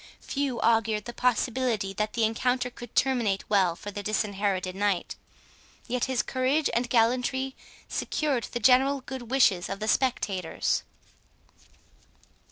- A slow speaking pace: Yes, slow, 130 wpm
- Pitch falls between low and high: No, high, 235 Hz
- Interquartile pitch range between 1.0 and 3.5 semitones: No, average, 3.9 semitones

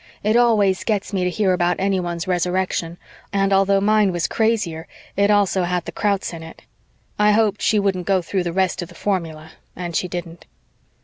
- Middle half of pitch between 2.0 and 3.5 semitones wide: Yes, narrow, 2.5 semitones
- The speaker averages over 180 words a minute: Yes, average, 190 wpm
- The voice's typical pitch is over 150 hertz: Yes, high, 190 Hz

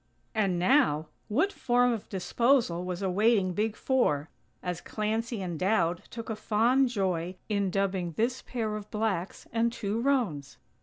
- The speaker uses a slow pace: No, average, 150 wpm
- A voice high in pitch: Yes, high, 210 Hz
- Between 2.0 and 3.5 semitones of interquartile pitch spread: No, average, 4.5 semitones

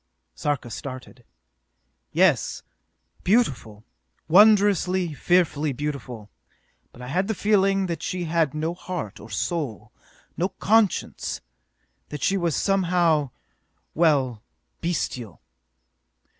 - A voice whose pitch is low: No, medium, 165 Hz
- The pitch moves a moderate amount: No, wide, 5.7 semitones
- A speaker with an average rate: No, slow, 100 wpm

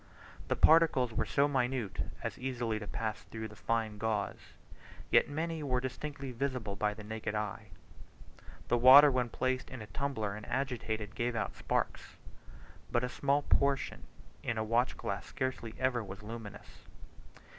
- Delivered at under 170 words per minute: Yes, average, 155 wpm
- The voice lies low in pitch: Yes, low, 120 Hz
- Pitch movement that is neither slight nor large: Yes, average, 3.4 semitones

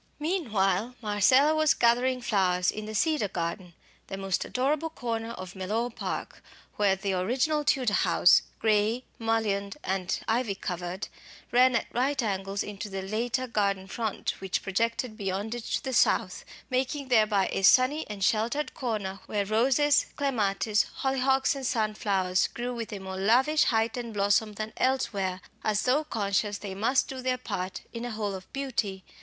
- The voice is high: Yes, high, 220 Hz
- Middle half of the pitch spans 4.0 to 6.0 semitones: Yes, average, 4.4 semitones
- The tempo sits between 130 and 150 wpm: No, average, 160 wpm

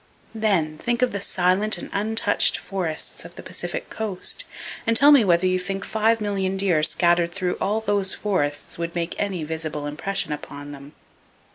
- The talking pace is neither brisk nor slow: Yes, average, 170 wpm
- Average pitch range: Yes, average, 3.9 semitones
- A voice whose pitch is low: No, high, 190 Hz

